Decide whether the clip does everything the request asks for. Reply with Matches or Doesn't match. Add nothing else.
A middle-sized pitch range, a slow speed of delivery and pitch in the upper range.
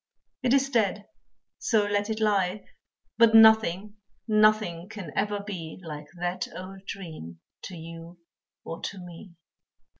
Matches